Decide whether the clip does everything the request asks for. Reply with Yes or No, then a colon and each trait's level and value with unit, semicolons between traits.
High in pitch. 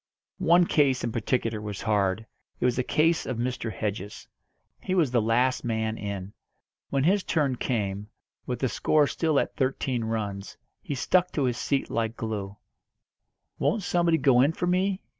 No: low, 125 Hz